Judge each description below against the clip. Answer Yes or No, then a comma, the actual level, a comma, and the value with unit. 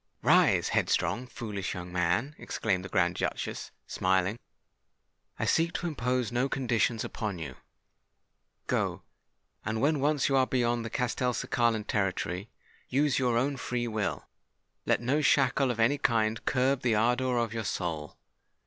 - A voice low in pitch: Yes, low, 120 Hz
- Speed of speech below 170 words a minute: Yes, average, 140 wpm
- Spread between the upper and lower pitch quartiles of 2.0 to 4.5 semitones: Yes, average, 3.8 semitones